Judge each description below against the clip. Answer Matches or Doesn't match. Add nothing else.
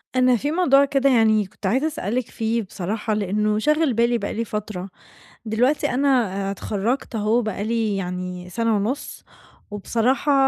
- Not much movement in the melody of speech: Doesn't match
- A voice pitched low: Doesn't match